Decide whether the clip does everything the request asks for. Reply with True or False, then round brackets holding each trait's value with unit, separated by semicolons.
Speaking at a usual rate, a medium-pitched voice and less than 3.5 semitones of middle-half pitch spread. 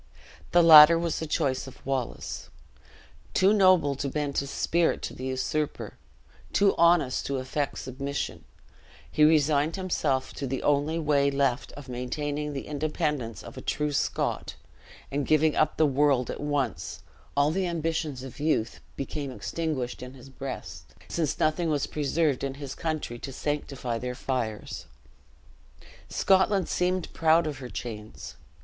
True (150 wpm; 145 Hz; 3.1 semitones)